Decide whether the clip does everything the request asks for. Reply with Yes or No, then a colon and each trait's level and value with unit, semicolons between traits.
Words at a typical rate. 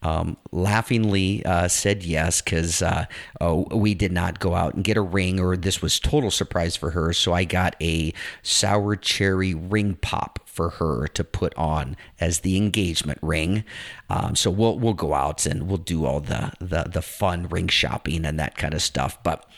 Yes: average, 195 wpm